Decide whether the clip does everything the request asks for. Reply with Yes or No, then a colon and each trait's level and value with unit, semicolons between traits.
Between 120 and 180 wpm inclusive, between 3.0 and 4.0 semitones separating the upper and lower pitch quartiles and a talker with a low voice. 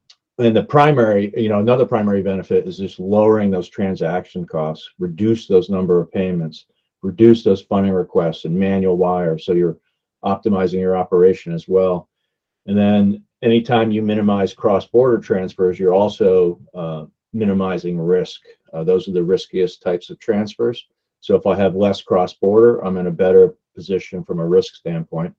Yes: average, 170 wpm; average, 3.7 semitones; very low, 95 Hz